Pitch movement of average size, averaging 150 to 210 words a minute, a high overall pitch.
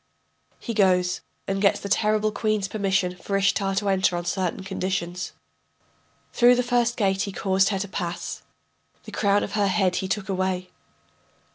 No: narrow, 1.8 semitones; average, 165 wpm; high, 195 Hz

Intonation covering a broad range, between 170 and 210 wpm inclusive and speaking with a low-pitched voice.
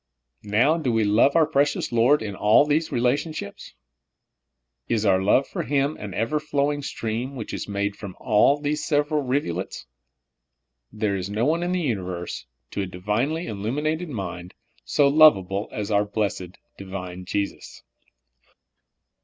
No: wide, 6.5 semitones; average, 150 wpm; low, 115 Hz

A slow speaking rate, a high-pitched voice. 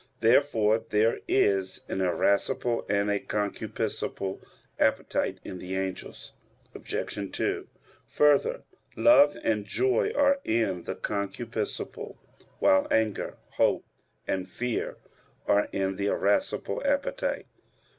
No: slow, 105 wpm; low, 105 Hz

